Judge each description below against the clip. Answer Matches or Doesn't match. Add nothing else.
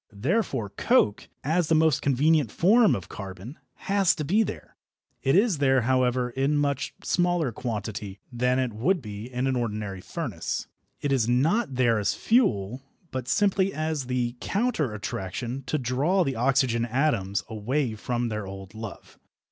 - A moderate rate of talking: Matches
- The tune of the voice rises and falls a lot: Matches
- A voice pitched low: Matches